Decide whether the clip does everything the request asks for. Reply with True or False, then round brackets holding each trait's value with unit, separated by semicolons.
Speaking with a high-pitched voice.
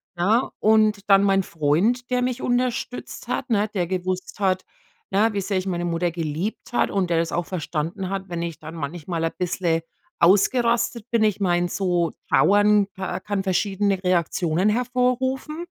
True (195 Hz)